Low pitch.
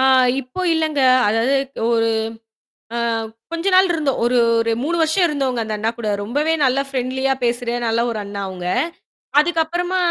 No: very high, 265 Hz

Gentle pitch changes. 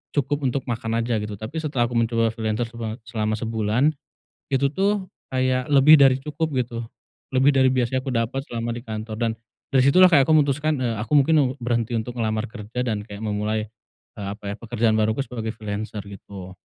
No: average, 3.6 semitones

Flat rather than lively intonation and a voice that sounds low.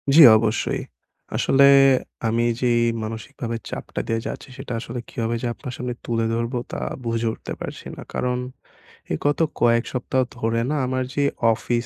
Yes: narrow, 1.8 semitones; low, 120 Hz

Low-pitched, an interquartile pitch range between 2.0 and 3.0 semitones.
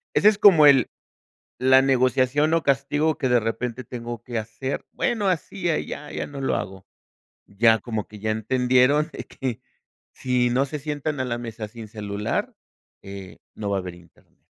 No: low, 125 Hz; average, 4.5 semitones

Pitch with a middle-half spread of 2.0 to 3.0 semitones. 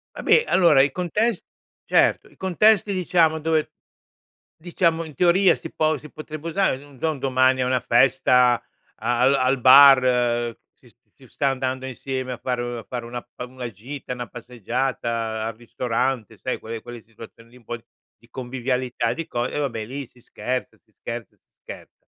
No: average, 3.9 semitones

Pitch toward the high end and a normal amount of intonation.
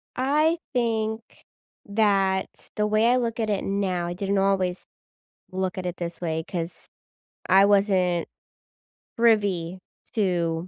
Yes: high, 195 Hz; average, 3.4 semitones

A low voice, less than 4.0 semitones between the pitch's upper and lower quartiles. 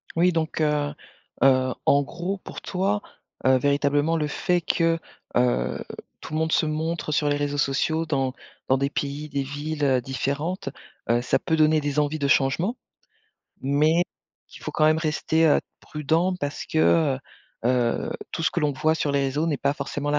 No: medium, 150 Hz; narrow, 2.4 semitones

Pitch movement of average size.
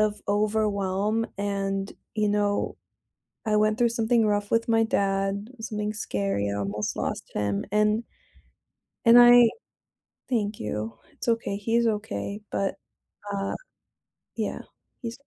No: narrow, 2.2 semitones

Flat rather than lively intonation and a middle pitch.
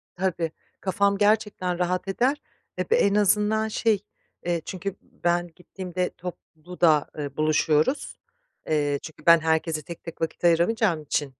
No: average, 3.9 semitones; medium, 175 Hz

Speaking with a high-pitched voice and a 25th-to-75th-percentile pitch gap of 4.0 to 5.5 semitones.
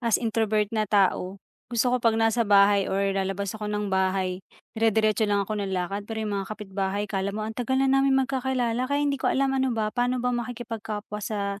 No: high, 215 Hz; average, 3.3 semitones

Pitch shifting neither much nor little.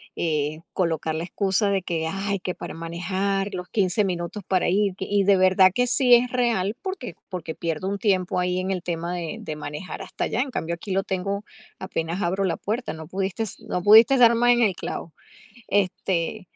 Yes: average, 3.0 semitones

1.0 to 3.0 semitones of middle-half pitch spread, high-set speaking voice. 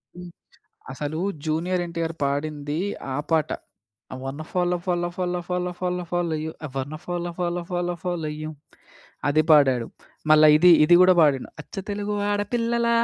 No: average, 2.7 semitones; medium, 175 Hz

